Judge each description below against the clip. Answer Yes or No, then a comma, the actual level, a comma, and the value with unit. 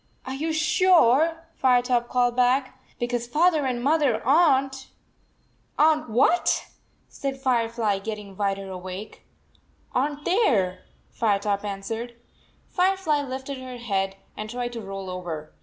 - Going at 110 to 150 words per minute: Yes, average, 145 wpm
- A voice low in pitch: No, high, 245 Hz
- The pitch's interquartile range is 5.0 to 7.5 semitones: Yes, average, 5.3 semitones